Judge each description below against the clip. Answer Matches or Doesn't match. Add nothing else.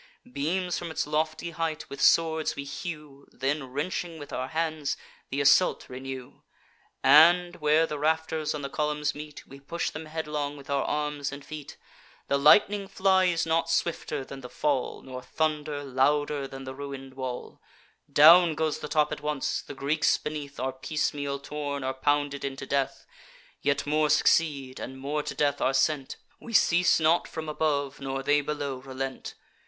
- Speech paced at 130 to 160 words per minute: Doesn't match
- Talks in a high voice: Doesn't match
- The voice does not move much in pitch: Matches